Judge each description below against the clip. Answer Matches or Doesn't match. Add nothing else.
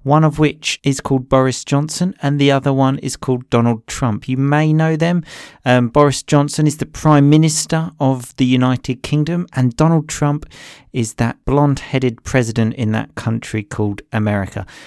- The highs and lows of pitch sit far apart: Doesn't match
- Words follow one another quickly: Doesn't match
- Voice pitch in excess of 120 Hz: Matches